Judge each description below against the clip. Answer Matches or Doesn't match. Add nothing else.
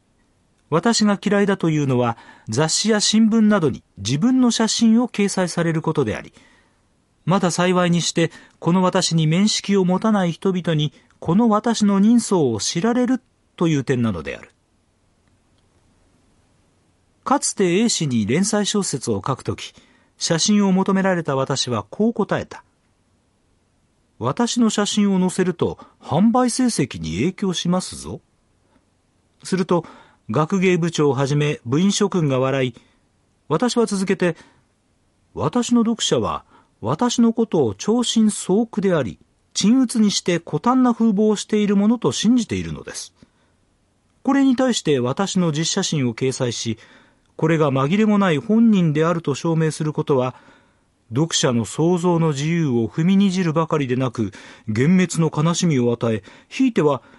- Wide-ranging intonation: Matches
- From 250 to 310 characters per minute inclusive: Matches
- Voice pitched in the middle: Matches